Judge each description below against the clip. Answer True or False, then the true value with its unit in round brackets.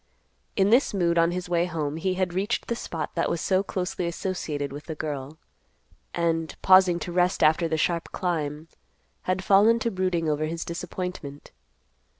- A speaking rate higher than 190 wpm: False (170 wpm)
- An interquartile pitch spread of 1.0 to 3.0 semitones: True (2.7 semitones)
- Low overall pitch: False (170 Hz)